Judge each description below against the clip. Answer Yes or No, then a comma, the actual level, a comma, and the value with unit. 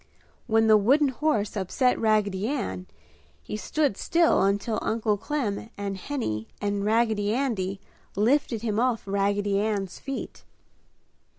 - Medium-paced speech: No, slow, 125 wpm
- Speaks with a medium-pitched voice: No, high, 215 Hz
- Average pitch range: Yes, average, 3.4 semitones